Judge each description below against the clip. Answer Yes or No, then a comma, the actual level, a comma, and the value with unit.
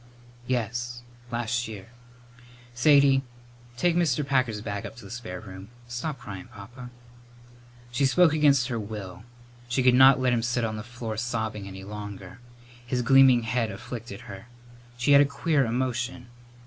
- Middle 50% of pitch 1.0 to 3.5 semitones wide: Yes, average, 3.2 semitones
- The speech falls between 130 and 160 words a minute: Yes, average, 155 wpm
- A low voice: Yes, low, 120 Hz